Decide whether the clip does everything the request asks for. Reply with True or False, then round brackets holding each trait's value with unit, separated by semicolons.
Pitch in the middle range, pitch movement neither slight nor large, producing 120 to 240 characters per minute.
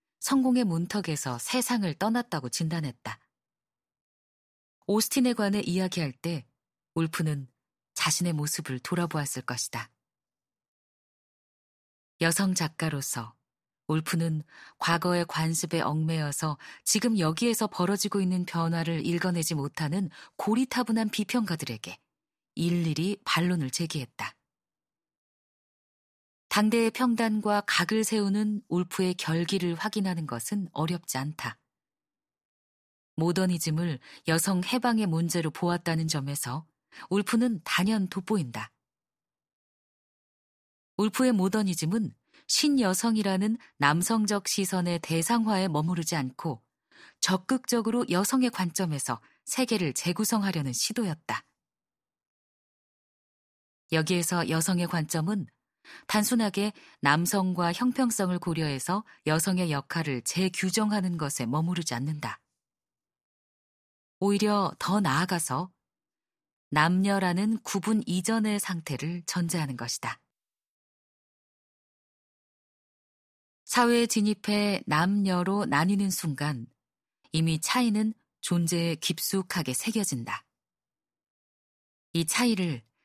True (175 Hz; 5.0 semitones; 235 characters per minute)